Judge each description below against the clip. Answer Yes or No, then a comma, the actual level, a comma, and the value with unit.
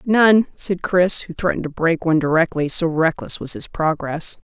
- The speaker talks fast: No, average, 185 wpm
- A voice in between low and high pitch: Yes, medium, 170 Hz